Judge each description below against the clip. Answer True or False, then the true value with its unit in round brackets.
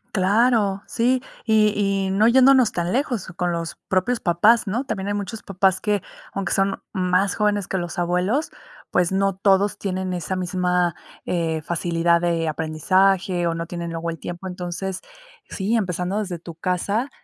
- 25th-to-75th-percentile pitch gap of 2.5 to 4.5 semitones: True (2.8 semitones)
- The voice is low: False (190 Hz)